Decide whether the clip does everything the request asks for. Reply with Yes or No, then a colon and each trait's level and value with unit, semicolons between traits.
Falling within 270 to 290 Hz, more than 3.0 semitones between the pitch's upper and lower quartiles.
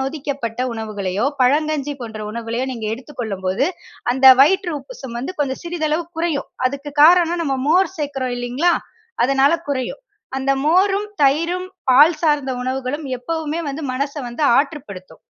Yes: very high, 280 Hz; average, 4.1 semitones